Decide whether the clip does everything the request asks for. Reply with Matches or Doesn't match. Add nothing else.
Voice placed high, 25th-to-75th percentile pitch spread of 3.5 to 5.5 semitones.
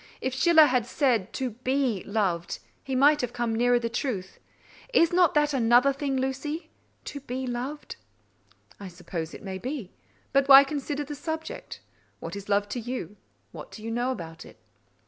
Matches